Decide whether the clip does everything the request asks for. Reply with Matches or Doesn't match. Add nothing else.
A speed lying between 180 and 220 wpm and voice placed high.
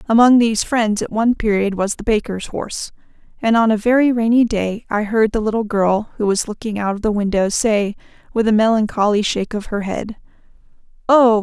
Matches